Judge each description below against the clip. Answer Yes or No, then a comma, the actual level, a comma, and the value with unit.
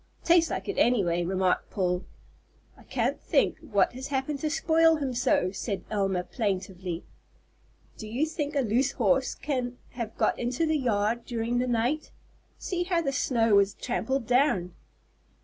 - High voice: Yes, high, 245 Hz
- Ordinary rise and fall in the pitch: No, wide, 5.8 semitones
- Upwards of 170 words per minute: No, average, 165 wpm